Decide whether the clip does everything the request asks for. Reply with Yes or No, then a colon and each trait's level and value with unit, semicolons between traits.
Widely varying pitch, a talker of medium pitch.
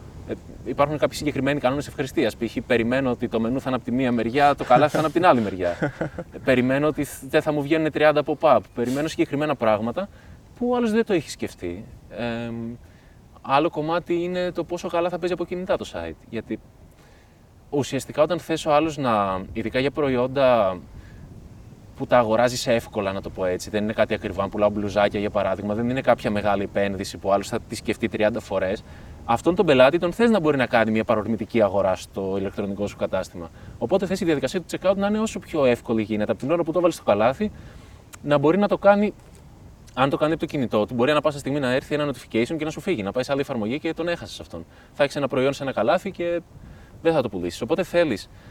No: wide, 6.8 semitones; low, 125 Hz